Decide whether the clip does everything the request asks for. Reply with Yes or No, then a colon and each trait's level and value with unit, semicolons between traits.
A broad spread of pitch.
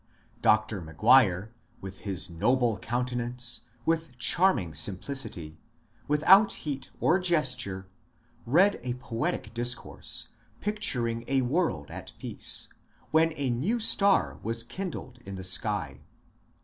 Yes: wide, 6.7 semitones